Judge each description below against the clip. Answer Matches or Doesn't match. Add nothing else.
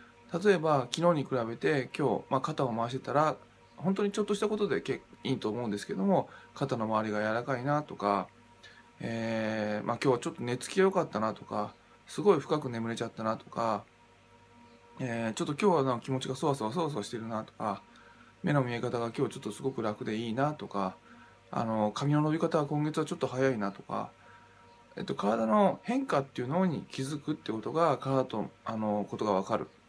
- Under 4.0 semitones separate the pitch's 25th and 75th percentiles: Doesn't match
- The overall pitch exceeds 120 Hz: Matches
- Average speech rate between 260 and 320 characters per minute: Doesn't match